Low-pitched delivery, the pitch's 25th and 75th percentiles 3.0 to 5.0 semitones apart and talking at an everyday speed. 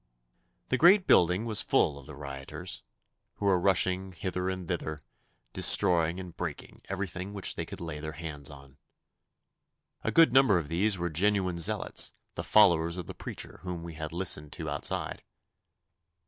Yes: very low, 90 Hz; average, 3.5 semitones; average, 160 wpm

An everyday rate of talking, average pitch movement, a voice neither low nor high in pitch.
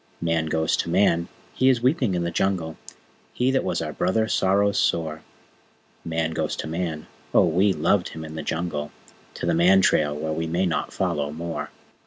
No: average, 190 wpm; average, 3.2 semitones; very low, 85 Hz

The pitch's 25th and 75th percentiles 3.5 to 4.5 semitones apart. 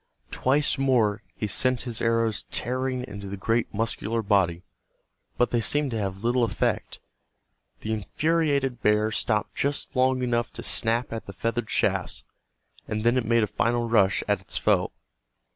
No: average, 3.1 semitones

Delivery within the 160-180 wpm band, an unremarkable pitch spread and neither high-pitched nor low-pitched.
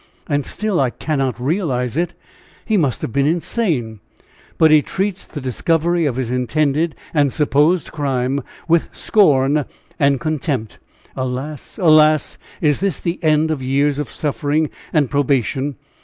No: average, 140 wpm; average, 3.2 semitones; medium, 145 Hz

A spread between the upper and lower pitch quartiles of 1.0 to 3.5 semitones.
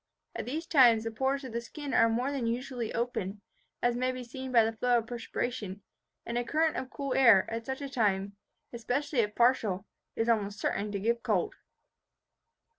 Yes: average, 2.8 semitones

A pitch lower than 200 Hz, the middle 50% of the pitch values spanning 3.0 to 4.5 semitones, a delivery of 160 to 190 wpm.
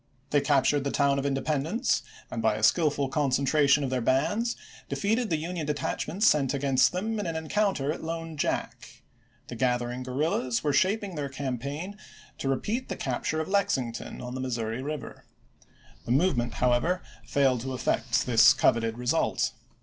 Yes: medium, 140 Hz; average, 4.2 semitones; average, 175 wpm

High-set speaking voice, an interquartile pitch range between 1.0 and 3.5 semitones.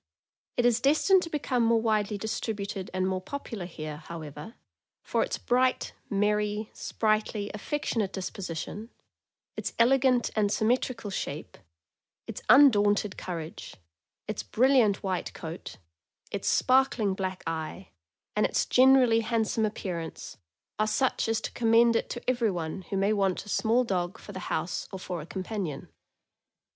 No: high, 210 Hz; average, 4.0 semitones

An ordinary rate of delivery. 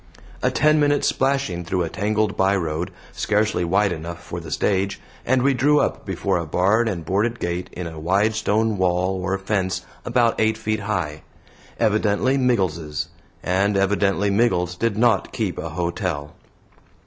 Yes: average, 160 wpm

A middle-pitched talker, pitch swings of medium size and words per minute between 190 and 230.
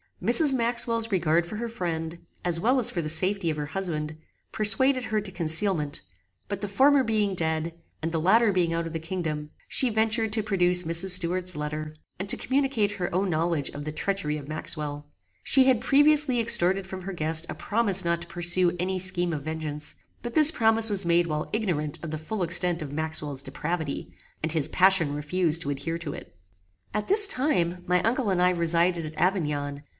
Yes: medium, 175 Hz; average, 4.9 semitones; average, 195 wpm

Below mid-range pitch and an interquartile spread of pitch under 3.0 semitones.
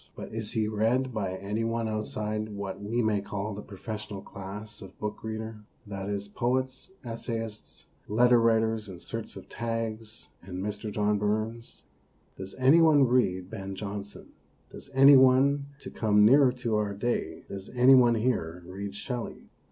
Yes: low, 110 Hz; narrow, 2.6 semitones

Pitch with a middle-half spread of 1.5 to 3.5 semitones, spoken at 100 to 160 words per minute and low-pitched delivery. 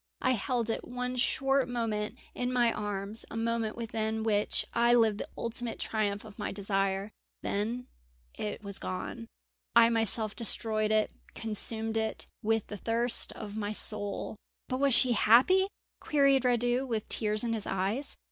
No: narrow, 2.4 semitones; average, 155 wpm; high, 225 Hz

